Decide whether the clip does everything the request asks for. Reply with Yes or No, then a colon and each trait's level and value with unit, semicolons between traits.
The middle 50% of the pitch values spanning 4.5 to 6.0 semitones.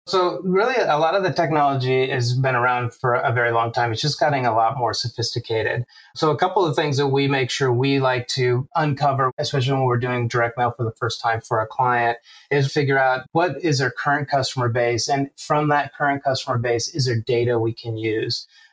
No: average, 3.2 semitones